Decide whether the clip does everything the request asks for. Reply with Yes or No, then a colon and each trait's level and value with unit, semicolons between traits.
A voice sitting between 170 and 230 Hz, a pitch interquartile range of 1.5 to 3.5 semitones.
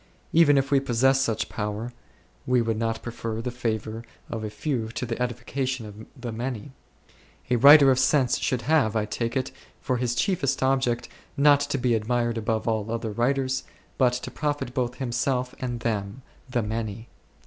No: low, 120 Hz; average, 2.7 semitones